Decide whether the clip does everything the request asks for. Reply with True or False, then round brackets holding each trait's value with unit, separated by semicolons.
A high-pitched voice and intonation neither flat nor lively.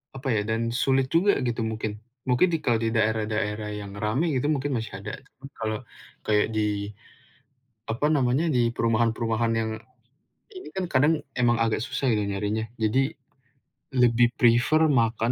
False (115 Hz; 3.1 semitones)